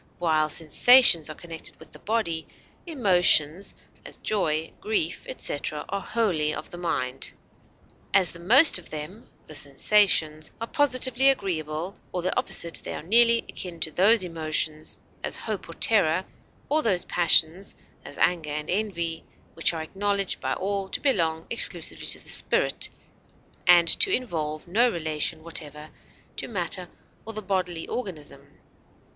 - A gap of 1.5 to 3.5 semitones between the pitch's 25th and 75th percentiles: No, average, 5.0 semitones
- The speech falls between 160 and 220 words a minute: No, average, 145 wpm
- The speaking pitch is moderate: Yes, medium, 175 Hz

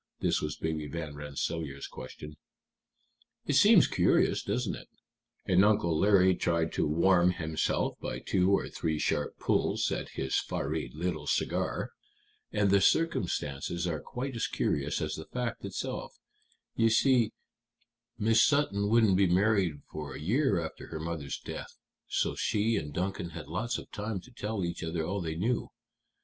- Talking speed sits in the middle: Yes, average, 160 wpm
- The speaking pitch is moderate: No, very low, 90 Hz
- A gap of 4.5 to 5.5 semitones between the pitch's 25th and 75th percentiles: Yes, average, 5.0 semitones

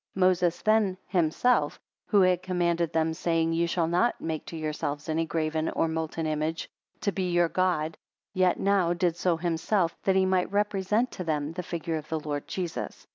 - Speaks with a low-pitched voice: No, medium, 170 Hz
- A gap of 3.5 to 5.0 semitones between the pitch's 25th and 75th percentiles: No, narrow, 2.5 semitones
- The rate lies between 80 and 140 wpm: No, average, 185 wpm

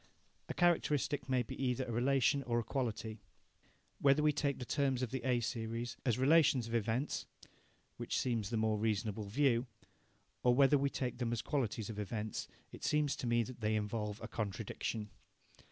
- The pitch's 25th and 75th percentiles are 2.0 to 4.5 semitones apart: Yes, average, 3.5 semitones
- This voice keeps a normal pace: Yes, average, 180 wpm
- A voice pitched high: No, low, 120 Hz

